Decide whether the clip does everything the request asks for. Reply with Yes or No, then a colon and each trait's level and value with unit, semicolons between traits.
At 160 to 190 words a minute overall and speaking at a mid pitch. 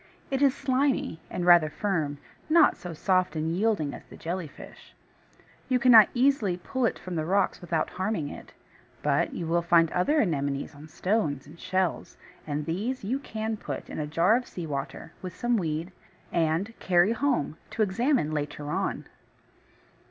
Yes: average, 170 wpm; medium, 180 Hz